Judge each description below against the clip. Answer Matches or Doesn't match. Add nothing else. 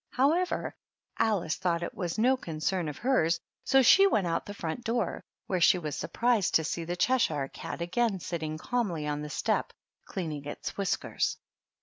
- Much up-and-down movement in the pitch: Matches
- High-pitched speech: Doesn't match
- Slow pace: Doesn't match